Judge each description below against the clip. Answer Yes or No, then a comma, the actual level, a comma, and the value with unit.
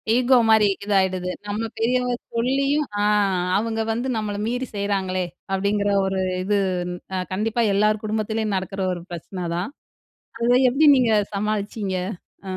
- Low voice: No, high, 210 Hz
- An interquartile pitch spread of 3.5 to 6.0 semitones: No, average, 3.1 semitones